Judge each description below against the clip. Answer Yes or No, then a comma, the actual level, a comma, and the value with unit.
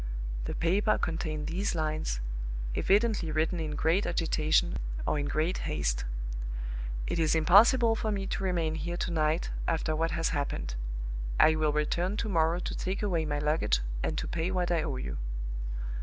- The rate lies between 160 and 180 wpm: Yes, average, 170 wpm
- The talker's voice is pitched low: No, medium, 165 Hz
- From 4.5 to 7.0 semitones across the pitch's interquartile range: No, average, 2.9 semitones